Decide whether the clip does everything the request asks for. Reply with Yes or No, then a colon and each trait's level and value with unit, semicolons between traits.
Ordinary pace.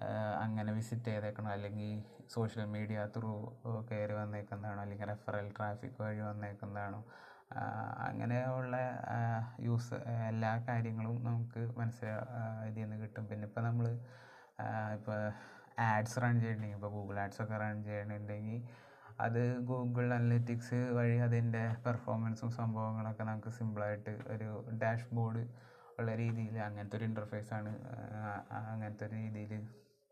Yes: average, 110 wpm